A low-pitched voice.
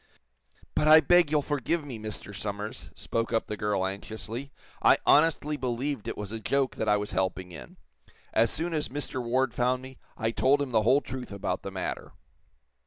Yes: low, 125 Hz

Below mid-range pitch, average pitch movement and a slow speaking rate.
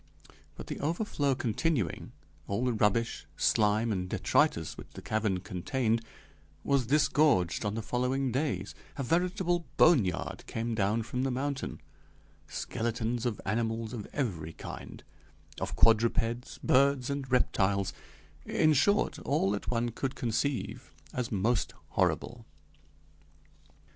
Yes: low, 120 Hz; average, 4.0 semitones; slow, 125 wpm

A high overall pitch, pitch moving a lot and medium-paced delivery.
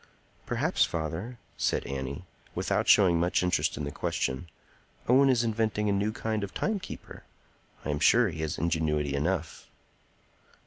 No: very low, 90 Hz; wide, 5.9 semitones; average, 145 wpm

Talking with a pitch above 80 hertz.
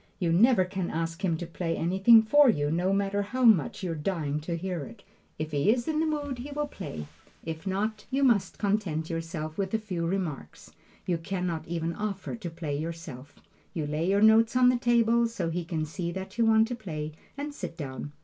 Yes: medium, 185 Hz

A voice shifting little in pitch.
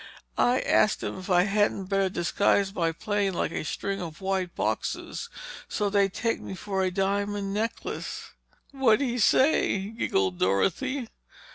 Yes: narrow, 2.3 semitones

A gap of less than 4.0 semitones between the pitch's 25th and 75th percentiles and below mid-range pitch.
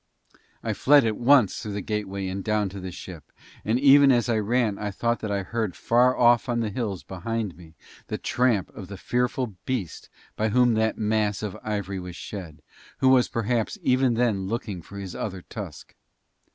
Yes: average, 3.6 semitones; low, 110 Hz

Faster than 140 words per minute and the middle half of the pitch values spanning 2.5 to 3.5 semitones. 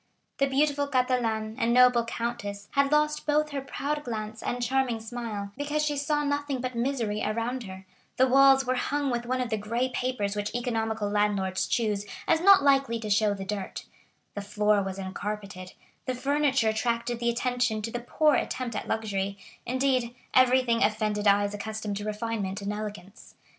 No: average, 175 wpm; average, 3.9 semitones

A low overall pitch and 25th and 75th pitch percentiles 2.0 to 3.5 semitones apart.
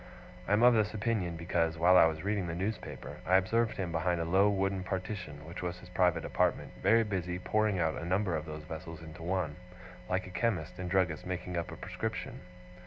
Yes: very low, 90 Hz; average, 2.8 semitones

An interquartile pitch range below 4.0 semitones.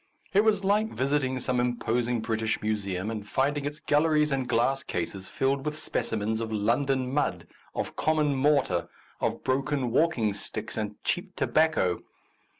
No: average, 5.0 semitones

